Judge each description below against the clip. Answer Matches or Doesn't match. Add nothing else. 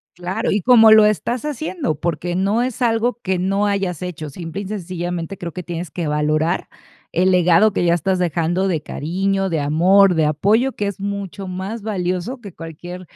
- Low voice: Doesn't match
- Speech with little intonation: Doesn't match